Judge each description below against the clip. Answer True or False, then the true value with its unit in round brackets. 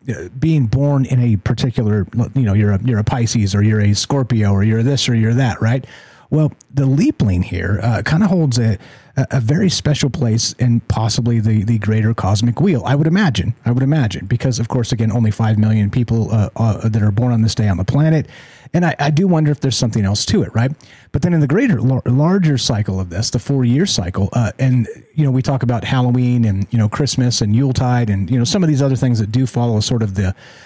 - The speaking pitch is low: True (120 Hz)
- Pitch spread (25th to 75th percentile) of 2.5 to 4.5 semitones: True (3.7 semitones)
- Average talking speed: False (235 wpm)